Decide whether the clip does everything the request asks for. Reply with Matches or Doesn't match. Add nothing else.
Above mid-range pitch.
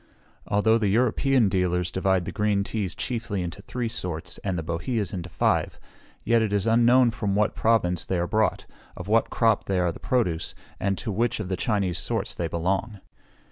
Doesn't match